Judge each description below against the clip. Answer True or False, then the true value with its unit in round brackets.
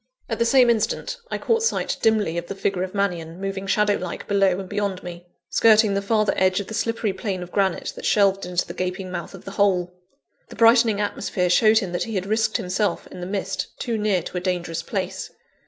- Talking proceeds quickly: True (220 wpm)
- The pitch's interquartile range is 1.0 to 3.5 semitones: True (3.0 semitones)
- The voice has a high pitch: True (195 Hz)